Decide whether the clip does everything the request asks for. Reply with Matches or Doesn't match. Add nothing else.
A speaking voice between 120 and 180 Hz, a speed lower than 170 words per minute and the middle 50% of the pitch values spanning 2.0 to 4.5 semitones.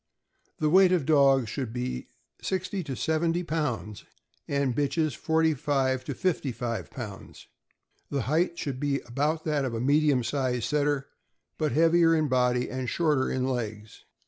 Matches